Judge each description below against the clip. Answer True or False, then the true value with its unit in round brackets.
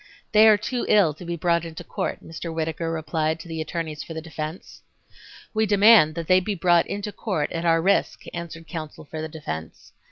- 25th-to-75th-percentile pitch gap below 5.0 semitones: True (2.6 semitones)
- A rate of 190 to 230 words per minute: True (200 wpm)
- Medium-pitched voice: True (165 Hz)